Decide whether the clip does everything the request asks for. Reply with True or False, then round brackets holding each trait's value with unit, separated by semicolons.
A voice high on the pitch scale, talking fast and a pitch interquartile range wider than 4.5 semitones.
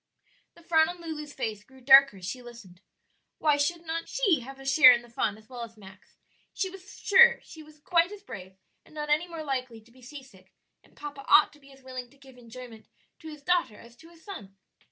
True (275 Hz; 230 wpm; 5.2 semitones)